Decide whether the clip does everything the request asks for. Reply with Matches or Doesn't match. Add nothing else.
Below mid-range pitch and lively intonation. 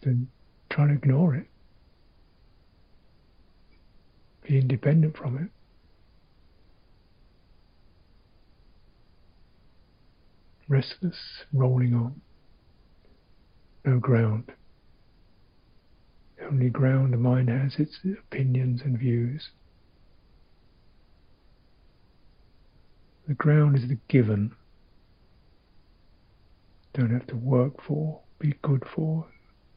Matches